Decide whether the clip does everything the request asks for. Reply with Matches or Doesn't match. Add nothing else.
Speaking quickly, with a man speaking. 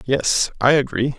Doesn't match